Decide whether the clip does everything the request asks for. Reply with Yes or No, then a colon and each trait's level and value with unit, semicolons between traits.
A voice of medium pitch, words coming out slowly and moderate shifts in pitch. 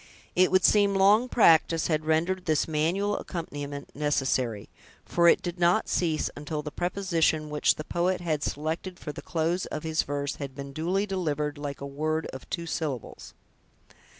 No: medium, 160 Hz; average, 170 wpm; average, 3.4 semitones